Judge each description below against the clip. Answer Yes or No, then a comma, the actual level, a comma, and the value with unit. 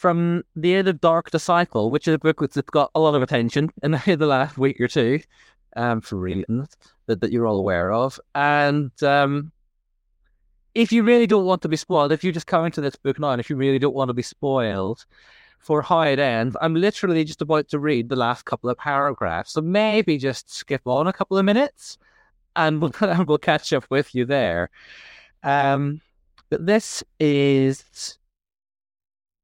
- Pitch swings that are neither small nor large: Yes, average, 4.1 semitones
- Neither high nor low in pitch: Yes, medium, 145 Hz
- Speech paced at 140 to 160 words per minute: No, average, 200 wpm